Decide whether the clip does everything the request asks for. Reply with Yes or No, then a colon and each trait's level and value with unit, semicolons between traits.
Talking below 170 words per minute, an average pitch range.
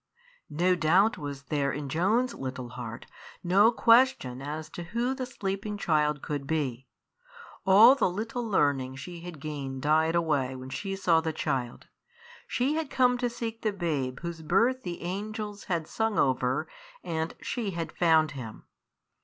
No: average, 160 wpm; wide, 6.8 semitones